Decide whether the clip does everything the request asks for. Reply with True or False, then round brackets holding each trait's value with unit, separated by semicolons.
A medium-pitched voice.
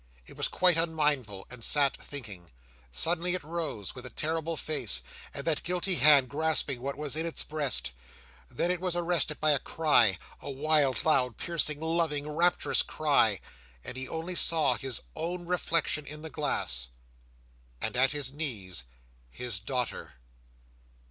True (150 Hz)